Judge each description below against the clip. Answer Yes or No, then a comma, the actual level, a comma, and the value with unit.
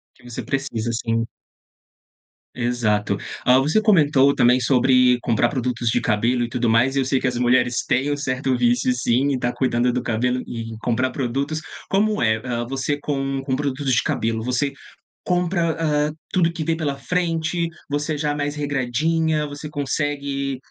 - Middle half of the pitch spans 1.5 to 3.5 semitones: Yes, average, 3.2 semitones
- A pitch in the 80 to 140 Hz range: Yes, low, 135 Hz